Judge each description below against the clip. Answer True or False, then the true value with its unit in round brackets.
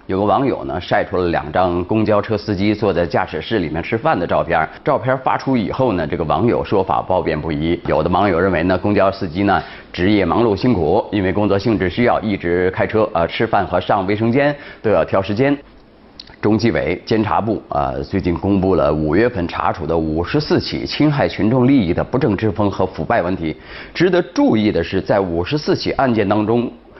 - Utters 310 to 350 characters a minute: True (315 characters per minute)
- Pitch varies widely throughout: False (3.9 semitones)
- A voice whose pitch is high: False (105 Hz)